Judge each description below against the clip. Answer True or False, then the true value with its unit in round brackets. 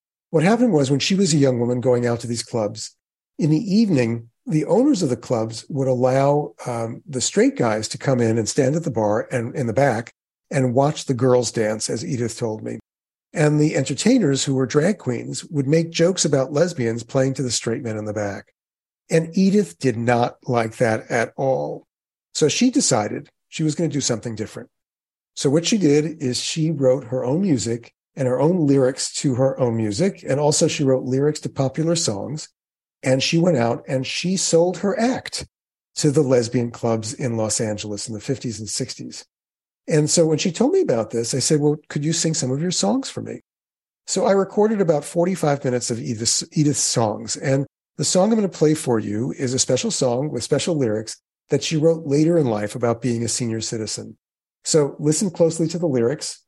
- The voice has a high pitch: False (135 Hz)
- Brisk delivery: True (210 wpm)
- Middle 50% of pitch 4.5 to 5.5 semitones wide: True (5.2 semitones)